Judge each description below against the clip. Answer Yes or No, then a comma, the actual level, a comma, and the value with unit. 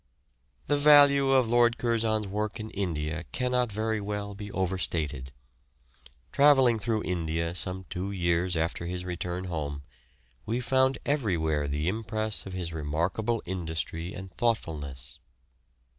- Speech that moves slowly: Yes, slow, 130 wpm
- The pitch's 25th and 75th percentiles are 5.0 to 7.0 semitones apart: Yes, wide, 5.5 semitones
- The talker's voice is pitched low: Yes, very low, 95 Hz